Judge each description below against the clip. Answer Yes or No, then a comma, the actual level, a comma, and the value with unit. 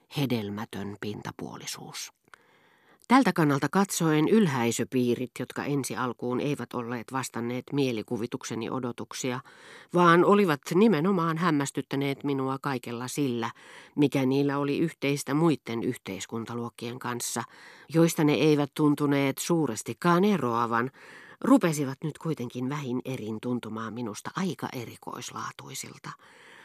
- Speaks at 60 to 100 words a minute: Yes, slow, 95 wpm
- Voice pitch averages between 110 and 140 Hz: Yes, low, 135 Hz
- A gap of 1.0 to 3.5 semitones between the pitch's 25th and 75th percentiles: No, average, 4.1 semitones